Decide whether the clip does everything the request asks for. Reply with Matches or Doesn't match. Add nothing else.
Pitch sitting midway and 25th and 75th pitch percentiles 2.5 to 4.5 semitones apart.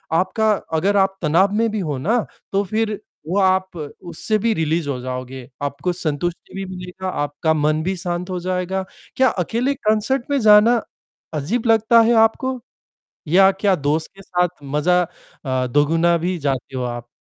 Doesn't match